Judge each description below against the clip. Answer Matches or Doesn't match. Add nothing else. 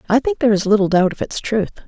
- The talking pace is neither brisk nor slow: Doesn't match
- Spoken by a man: Doesn't match